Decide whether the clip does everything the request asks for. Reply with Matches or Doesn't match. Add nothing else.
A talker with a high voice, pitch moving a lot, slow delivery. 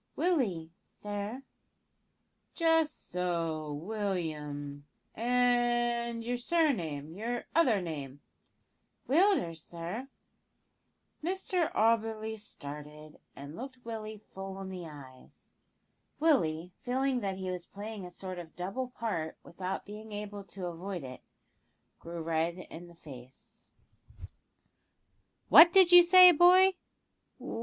Matches